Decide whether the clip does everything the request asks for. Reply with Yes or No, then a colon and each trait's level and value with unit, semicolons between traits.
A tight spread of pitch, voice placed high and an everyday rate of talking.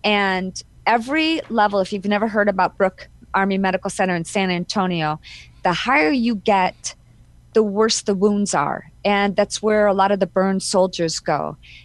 Yes: narrow, 2.1 semitones; high, 195 Hz; average, 170 wpm